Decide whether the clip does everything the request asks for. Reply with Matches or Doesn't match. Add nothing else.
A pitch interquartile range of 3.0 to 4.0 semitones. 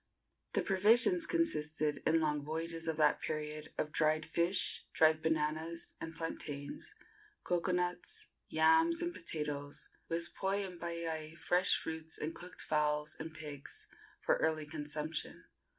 Doesn't match